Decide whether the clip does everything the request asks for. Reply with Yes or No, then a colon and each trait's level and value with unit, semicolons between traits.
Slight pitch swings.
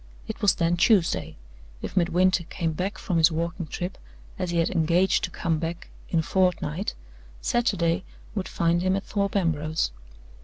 Yes: narrow, 2.2 semitones